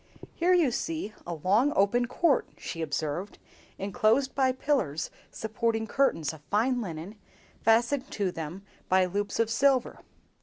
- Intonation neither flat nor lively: No, wide, 6.0 semitones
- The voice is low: No, high, 220 Hz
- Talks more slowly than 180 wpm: Yes, average, 140 wpm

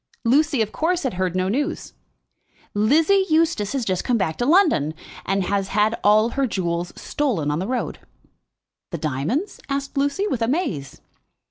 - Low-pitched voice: No, high, 225 Hz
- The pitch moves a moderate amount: No, wide, 7.6 semitones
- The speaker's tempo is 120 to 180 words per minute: Yes, average, 160 wpm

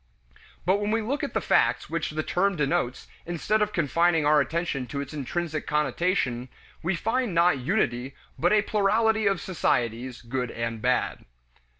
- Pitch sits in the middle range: Yes, medium, 165 Hz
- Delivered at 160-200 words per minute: Yes, average, 165 wpm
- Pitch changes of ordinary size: No, wide, 7.0 semitones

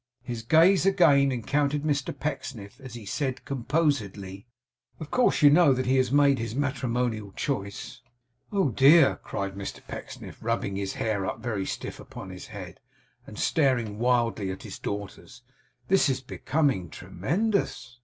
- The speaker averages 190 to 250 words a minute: No, average, 150 wpm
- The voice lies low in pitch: Yes, low, 125 Hz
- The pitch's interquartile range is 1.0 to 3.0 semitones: No, wide, 5.6 semitones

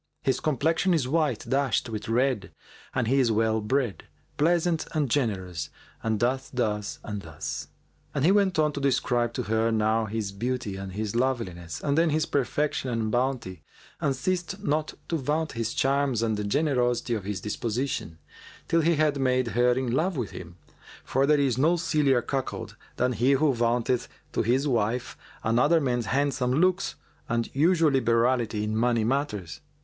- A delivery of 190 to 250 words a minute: No, average, 170 wpm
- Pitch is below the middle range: Yes, low, 125 Hz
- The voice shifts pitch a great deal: No, average, 4.3 semitones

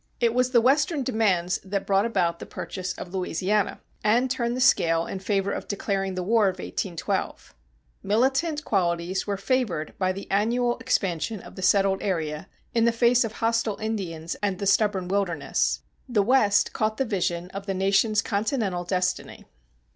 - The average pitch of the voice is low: No, high, 200 Hz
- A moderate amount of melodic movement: Yes, average, 3.8 semitones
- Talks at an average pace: Yes, average, 170 wpm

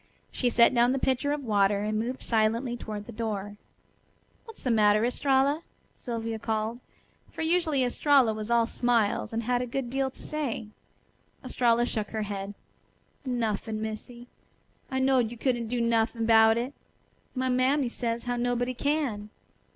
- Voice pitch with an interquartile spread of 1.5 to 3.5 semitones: Yes, average, 2.7 semitones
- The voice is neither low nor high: No, high, 235 Hz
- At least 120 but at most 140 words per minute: No, average, 160 wpm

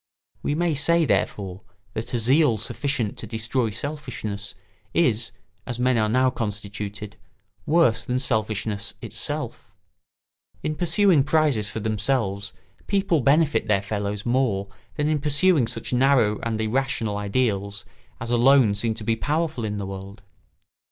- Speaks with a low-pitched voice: Yes, low, 115 Hz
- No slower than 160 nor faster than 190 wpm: No, average, 140 wpm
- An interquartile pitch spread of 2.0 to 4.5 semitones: No, average, 5.1 semitones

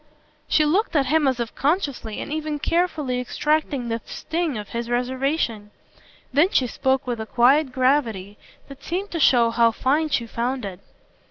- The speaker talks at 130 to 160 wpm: No, average, 170 wpm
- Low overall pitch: No, very high, 265 Hz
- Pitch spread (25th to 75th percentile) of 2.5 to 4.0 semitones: No, average, 4.4 semitones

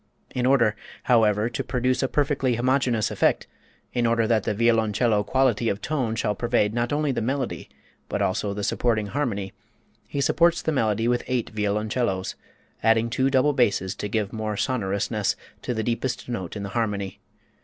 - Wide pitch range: No, average, 3.4 semitones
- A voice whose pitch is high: No, low, 115 Hz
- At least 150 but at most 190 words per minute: Yes, average, 170 wpm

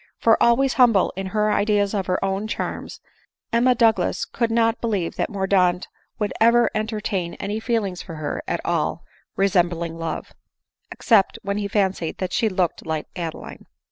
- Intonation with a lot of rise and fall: No, average, 3.6 semitones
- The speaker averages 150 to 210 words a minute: Yes, average, 165 wpm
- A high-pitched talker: Yes, high, 200 Hz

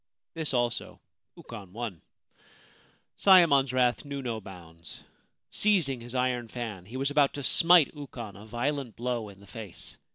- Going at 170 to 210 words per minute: No, average, 150 wpm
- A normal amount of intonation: Yes, average, 4.4 semitones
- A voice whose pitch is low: Yes, low, 120 Hz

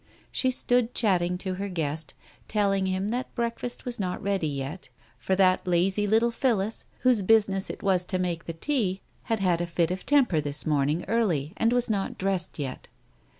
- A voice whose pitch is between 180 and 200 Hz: Yes, high, 190 Hz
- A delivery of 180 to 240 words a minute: Yes, average, 190 wpm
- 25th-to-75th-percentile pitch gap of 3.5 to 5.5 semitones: Yes, average, 4.5 semitones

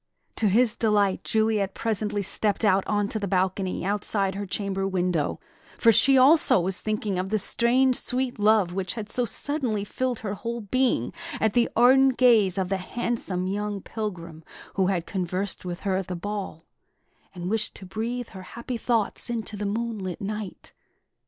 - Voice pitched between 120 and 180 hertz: No, high, 205 Hz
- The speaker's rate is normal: Yes, average, 170 wpm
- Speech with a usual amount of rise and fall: Yes, average, 3.3 semitones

